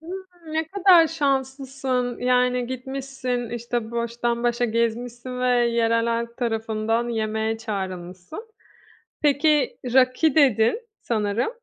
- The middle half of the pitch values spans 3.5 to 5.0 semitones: No, average, 2.8 semitones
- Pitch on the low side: No, high, 245 Hz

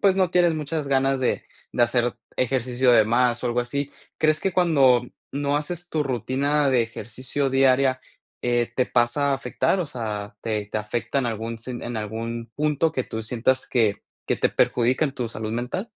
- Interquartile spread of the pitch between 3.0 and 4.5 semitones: Yes, average, 3.4 semitones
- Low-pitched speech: Yes, low, 125 Hz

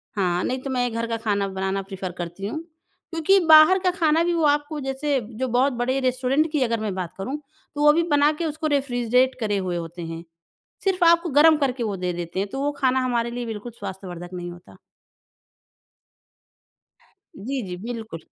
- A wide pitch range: Yes, wide, 6.9 semitones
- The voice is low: No, high, 245 Hz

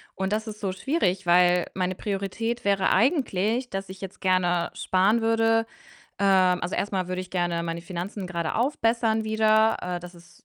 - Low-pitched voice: No, high, 195 Hz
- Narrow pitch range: No, average, 3.5 semitones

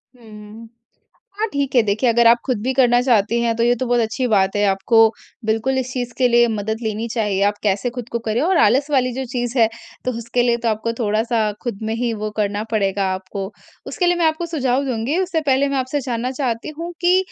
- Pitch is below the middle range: No, high, 235 Hz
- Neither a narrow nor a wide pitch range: Yes, average, 3.2 semitones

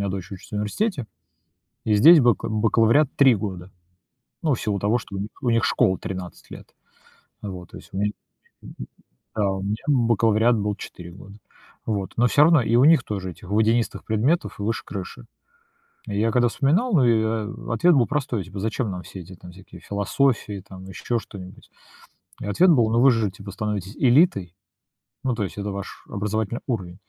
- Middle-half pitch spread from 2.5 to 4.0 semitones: Yes, average, 3.7 semitones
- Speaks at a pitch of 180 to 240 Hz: No, low, 110 Hz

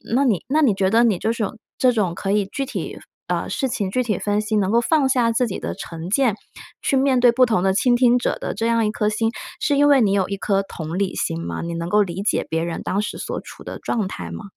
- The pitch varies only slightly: No, average, 4.4 semitones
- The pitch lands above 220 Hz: No, high, 215 Hz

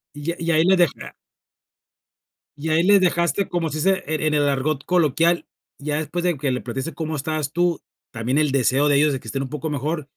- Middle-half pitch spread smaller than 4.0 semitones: Yes, average, 3.1 semitones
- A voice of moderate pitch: Yes, medium, 155 Hz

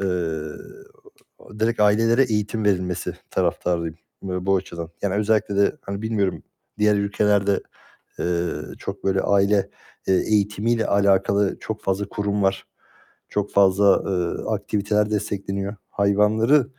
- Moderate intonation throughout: No, narrow, 1.6 semitones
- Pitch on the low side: Yes, low, 100 Hz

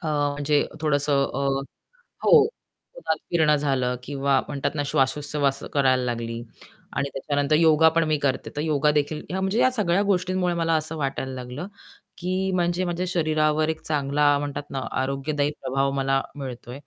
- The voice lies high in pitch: No, medium, 150 Hz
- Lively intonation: No, average, 3.1 semitones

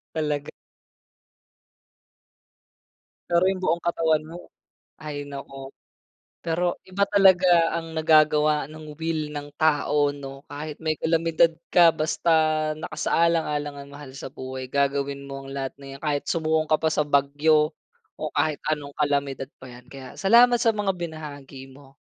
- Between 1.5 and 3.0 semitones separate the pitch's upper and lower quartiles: Yes, narrow, 2.6 semitones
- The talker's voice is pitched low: No, medium, 150 Hz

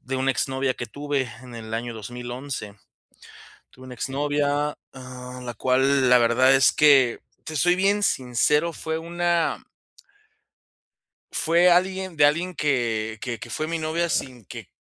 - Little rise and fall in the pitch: No, average, 4.2 semitones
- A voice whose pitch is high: No, low, 135 Hz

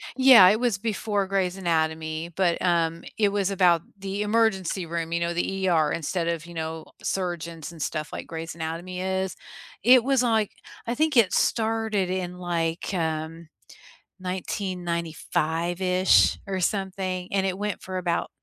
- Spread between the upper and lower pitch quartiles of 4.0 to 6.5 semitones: No, average, 2.8 semitones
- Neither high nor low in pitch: Yes, medium, 180 Hz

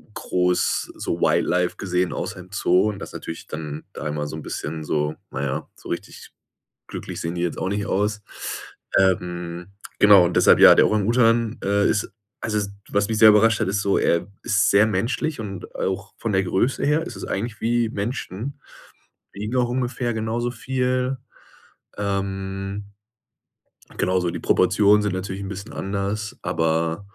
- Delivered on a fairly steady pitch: No, average, 3.6 semitones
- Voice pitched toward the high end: No, low, 100 Hz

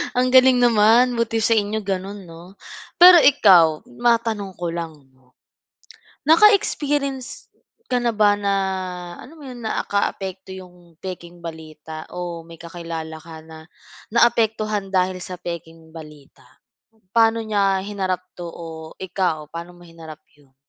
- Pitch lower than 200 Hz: Yes, high, 190 Hz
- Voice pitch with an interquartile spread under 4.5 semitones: No, average, 5.3 semitones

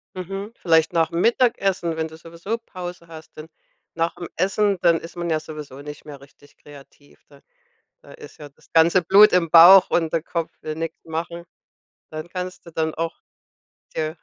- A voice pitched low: No, medium, 165 Hz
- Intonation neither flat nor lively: No, narrow, 2.3 semitones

